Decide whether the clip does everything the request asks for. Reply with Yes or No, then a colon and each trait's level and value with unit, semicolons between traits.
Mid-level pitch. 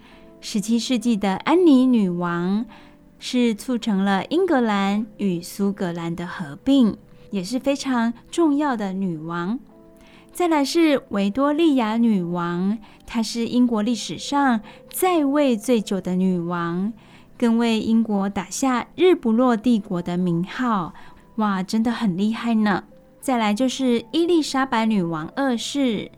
No: high, 225 Hz